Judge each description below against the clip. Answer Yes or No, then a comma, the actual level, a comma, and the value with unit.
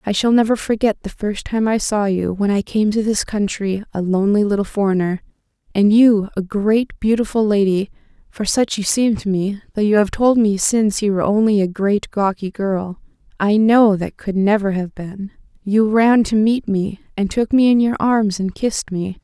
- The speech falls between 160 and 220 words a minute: Yes, average, 195 wpm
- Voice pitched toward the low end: No, high, 205 Hz